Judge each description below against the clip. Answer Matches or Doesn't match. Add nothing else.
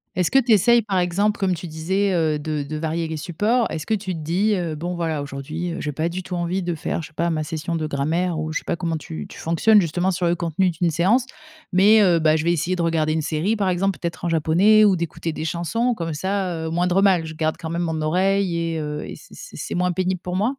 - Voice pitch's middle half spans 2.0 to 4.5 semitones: Matches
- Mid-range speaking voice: Matches